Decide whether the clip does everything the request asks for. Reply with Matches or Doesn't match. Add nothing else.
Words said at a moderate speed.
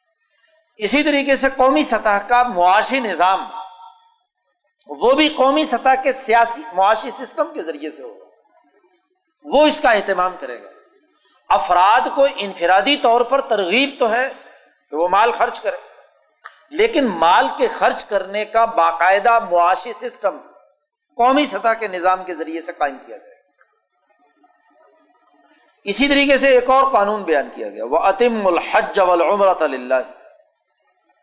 Matches